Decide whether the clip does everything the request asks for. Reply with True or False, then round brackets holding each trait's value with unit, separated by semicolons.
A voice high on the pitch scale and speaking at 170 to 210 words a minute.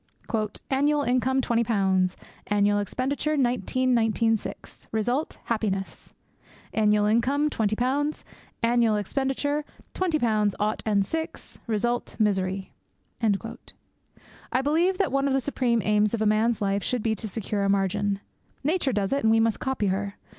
False (225 Hz; 145 wpm)